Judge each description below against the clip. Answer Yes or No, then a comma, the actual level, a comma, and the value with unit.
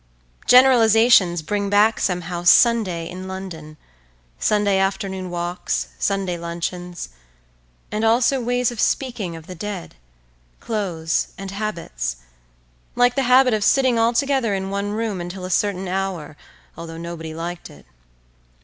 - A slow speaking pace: Yes, slow, 130 wpm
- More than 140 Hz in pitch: Yes, high, 190 Hz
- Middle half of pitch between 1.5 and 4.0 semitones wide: No, average, 4.5 semitones